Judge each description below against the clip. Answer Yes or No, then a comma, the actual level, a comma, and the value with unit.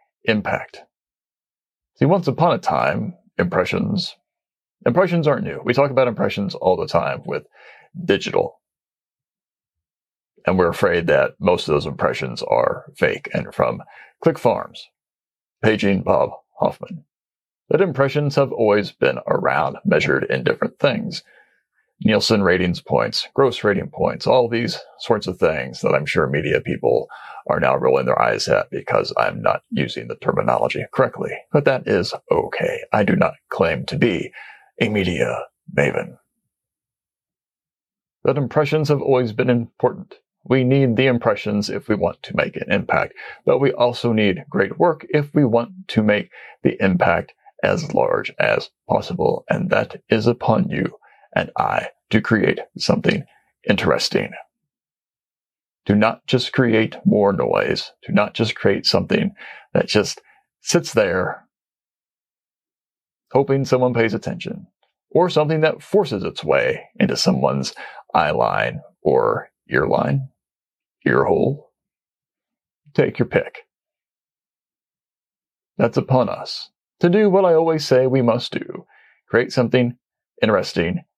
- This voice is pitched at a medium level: No, low, 130 Hz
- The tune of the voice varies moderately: No, wide, 7.2 semitones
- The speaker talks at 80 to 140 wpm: Yes, slow, 135 wpm